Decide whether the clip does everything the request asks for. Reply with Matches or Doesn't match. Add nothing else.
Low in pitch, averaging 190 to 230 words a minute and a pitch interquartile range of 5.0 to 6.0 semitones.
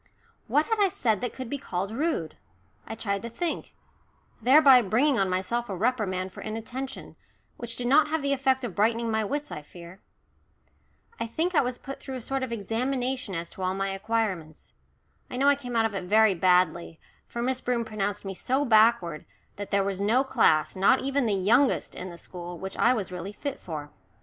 Doesn't match